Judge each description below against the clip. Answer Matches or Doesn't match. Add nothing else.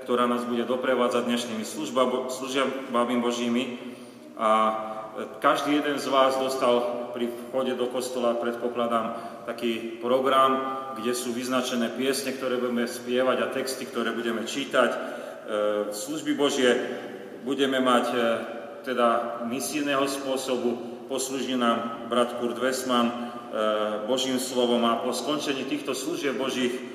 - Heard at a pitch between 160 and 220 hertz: Doesn't match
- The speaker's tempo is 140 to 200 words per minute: Doesn't match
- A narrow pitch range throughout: Matches